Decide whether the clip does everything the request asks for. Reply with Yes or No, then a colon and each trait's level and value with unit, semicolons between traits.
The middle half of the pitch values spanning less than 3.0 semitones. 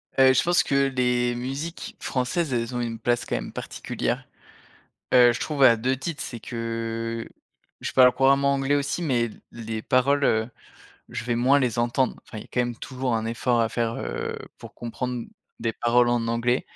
Yes: narrow, 2.4 semitones